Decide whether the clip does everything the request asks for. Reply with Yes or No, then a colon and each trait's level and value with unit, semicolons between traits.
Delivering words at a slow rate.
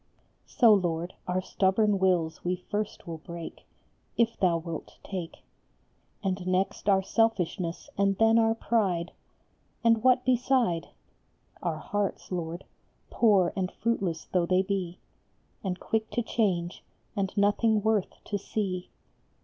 Yes: slow, 130 wpm